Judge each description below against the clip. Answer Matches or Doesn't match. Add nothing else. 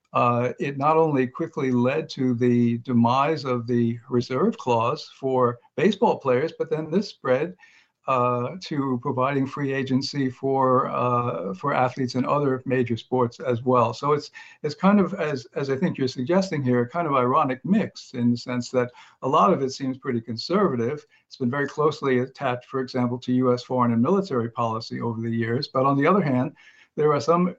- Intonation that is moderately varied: Matches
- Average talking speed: Matches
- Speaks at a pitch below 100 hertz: Doesn't match